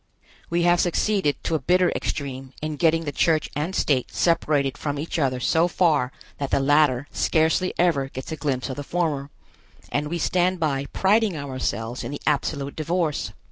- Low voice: No, medium, 150 Hz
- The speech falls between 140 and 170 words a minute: No, average, 180 wpm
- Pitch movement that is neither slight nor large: Yes, average, 3.6 semitones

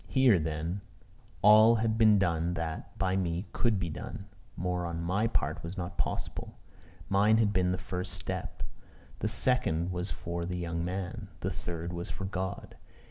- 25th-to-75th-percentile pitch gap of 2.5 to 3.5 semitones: Yes, average, 3.0 semitones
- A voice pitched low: Yes, very low, 90 Hz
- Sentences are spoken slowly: No, average, 170 wpm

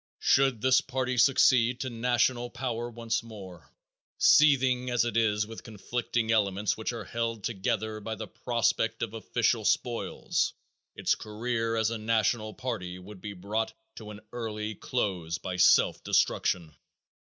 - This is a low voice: Yes, low, 115 Hz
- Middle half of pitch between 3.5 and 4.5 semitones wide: No, narrow, 2.4 semitones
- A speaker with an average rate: Yes, average, 145 wpm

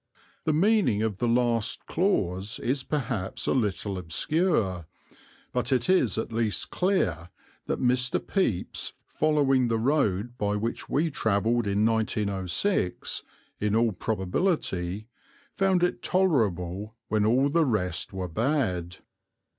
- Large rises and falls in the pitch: Yes, wide, 6.1 semitones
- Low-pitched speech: Yes, low, 115 Hz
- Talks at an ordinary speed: No, slow, 125 wpm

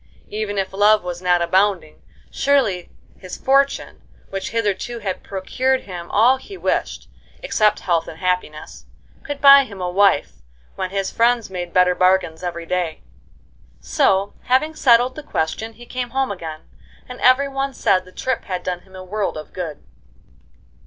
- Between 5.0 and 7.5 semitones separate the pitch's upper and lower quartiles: Yes, average, 5.3 semitones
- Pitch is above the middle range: Yes, high, 195 Hz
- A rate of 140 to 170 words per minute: Yes, average, 160 wpm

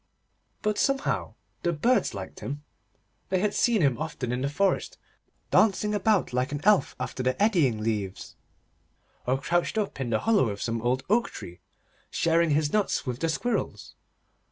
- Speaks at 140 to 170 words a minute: Yes, average, 165 wpm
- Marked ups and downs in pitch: Yes, wide, 8.5 semitones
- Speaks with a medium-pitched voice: Yes, medium, 155 Hz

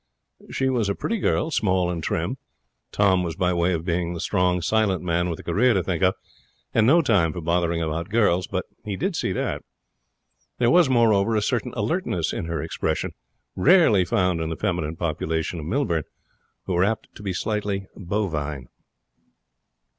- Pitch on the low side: Yes, very low, 95 Hz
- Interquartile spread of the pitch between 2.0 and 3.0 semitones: No, average, 4.3 semitones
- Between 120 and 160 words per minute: No, average, 175 wpm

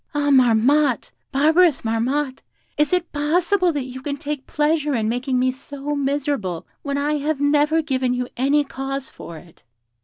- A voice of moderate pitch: No, very high, 280 Hz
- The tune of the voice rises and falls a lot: No, narrow, 2.5 semitones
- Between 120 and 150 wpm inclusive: No, average, 160 wpm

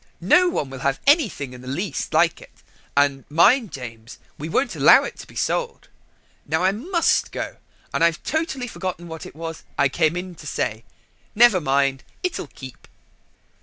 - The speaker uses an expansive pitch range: Yes, wide, 7.5 semitones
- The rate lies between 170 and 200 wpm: Yes, average, 175 wpm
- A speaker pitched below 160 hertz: No, medium, 165 Hz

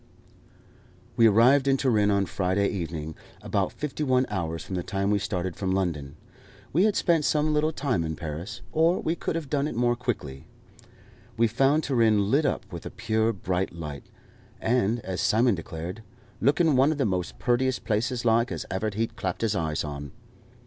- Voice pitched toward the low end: Yes, low, 110 Hz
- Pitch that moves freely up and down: Yes, wide, 6.1 semitones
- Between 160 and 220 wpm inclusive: Yes, average, 185 wpm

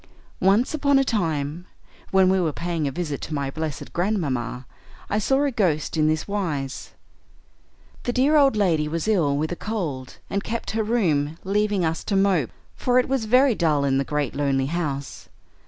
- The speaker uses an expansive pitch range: Yes, wide, 6.5 semitones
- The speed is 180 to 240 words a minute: Yes, average, 185 wpm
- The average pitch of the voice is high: No, medium, 175 Hz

